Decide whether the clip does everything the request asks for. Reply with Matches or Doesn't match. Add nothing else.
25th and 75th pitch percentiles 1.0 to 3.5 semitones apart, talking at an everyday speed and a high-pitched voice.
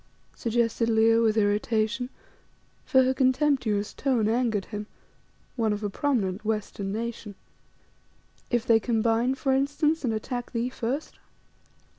Doesn't match